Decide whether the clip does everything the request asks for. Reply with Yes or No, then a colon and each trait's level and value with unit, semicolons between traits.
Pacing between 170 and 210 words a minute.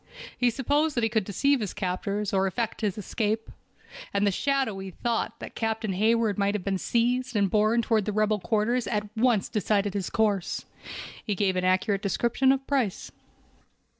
Yes: average, 175 wpm